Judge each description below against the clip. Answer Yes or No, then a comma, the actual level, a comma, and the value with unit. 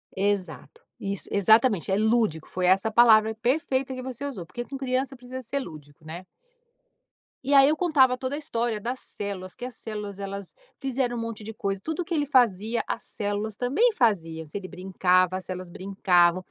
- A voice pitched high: Yes, high, 220 Hz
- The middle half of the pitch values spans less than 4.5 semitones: No, average, 5.3 semitones